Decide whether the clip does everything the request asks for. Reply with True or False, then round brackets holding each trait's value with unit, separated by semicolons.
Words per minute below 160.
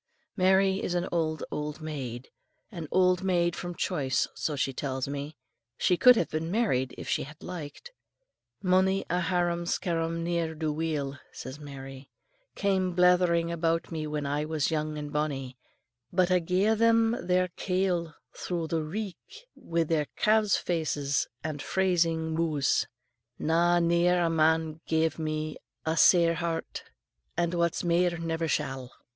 True (150 wpm)